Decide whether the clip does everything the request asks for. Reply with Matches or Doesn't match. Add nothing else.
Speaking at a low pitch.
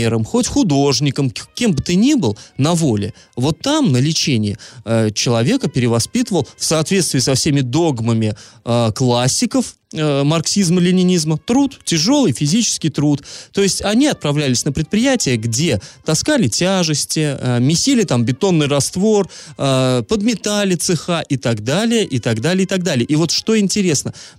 Doesn't match